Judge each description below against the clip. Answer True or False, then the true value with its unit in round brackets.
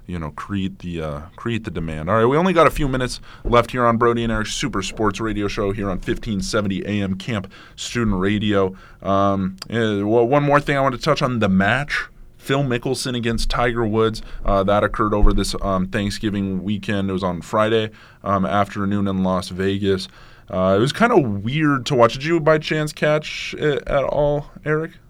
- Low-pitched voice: True (110 Hz)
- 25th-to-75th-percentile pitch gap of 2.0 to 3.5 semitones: False (4.2 semitones)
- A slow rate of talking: False (200 wpm)